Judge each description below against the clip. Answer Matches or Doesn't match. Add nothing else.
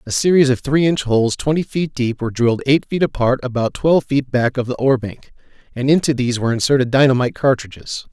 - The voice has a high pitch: Doesn't match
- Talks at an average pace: Doesn't match